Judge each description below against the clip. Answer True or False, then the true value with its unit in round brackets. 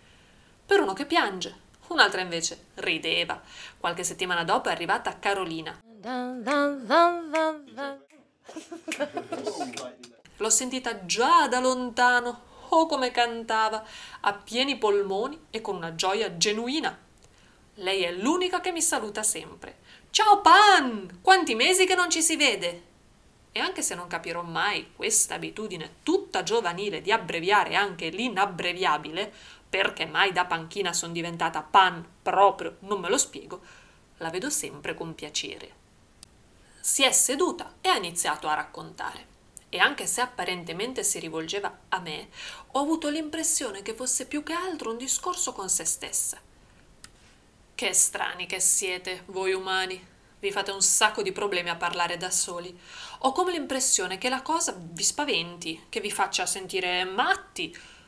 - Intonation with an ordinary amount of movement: False (8.4 semitones)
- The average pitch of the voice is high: True (220 Hz)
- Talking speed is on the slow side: False (140 wpm)